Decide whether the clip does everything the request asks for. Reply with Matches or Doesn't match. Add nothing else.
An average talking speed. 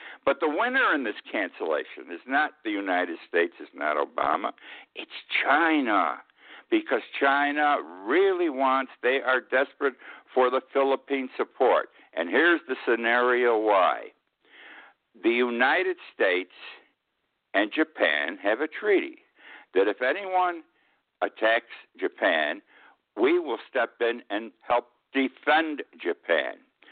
Doesn't match